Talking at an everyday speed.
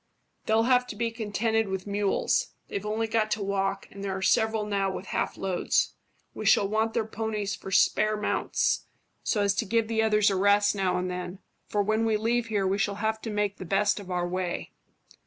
No: fast, 210 wpm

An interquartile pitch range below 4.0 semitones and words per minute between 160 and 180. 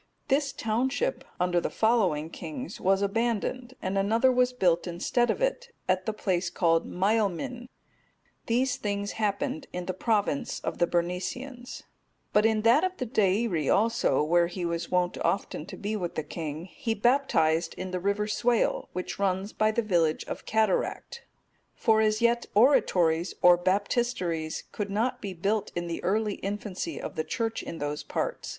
No: average, 4.9 semitones; average, 165 wpm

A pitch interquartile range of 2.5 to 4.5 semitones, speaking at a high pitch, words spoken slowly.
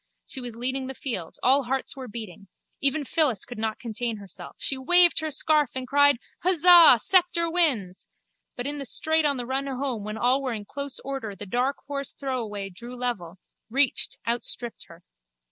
No: average, 4.0 semitones; very high, 260 Hz; average, 180 wpm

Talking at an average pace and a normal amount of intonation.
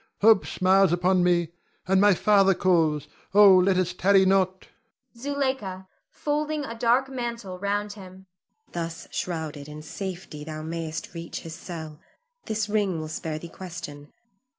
Yes: average, 145 wpm; average, 3.7 semitones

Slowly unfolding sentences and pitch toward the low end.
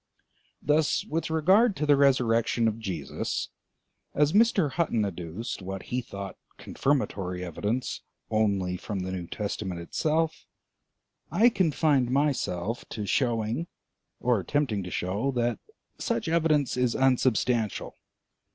Yes: slow, 120 wpm; low, 120 Hz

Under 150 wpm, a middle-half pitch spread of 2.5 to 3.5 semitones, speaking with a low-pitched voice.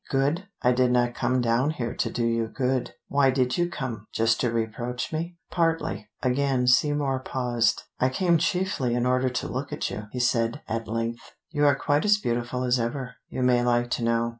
No: average, 200 wpm; average, 2.9 semitones; low, 125 Hz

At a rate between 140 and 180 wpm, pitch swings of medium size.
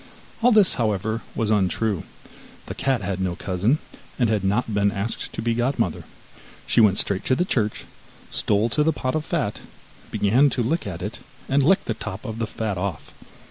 No: average, 190 wpm; average, 4.3 semitones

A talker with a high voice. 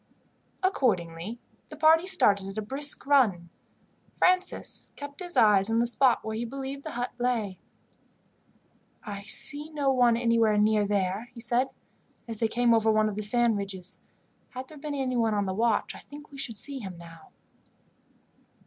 Yes: high, 230 Hz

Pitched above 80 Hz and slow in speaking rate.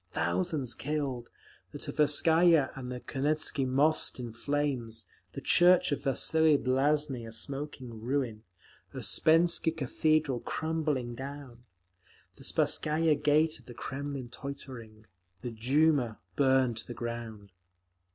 Yes: low, 135 Hz; slow, 115 wpm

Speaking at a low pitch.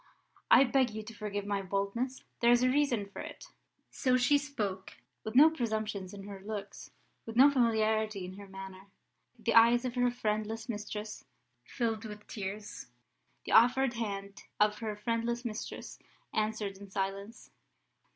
No: high, 220 Hz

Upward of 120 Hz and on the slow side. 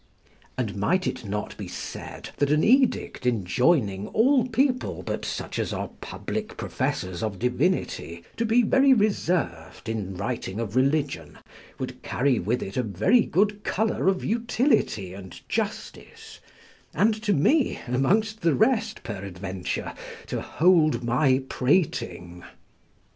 Yes: medium, 140 Hz; slow, 130 wpm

